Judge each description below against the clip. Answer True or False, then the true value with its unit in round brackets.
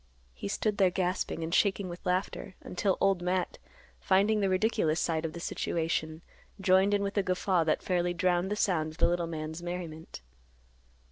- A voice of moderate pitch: True (180 Hz)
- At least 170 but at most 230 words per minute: True (180 wpm)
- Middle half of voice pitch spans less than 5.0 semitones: True (2.6 semitones)